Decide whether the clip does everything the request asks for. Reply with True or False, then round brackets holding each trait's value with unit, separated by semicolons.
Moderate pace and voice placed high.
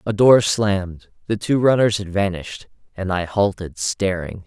False (160 wpm; 95 Hz)